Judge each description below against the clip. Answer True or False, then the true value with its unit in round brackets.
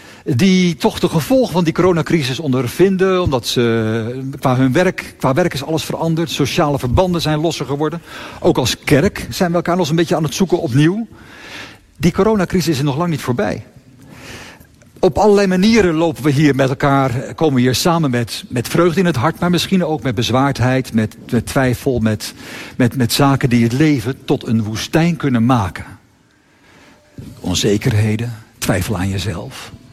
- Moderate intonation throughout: False (5.7 semitones)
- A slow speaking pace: False (170 wpm)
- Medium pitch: True (145 Hz)